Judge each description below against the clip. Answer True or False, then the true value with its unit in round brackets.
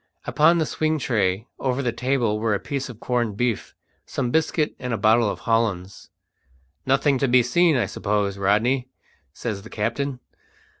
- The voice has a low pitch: True (120 Hz)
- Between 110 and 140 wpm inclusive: False (165 wpm)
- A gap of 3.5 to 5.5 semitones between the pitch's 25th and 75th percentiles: True (4.3 semitones)